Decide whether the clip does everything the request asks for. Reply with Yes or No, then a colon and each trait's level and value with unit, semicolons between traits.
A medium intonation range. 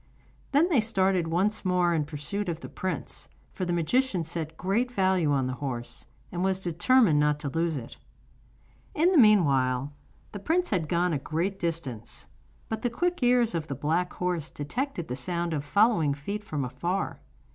No: wide, 5.8 semitones